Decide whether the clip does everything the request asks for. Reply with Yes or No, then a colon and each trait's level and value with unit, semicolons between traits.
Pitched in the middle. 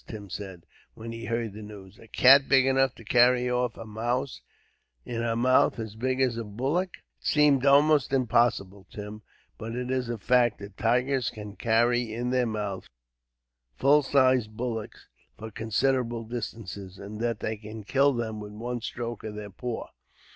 No: low, 115 Hz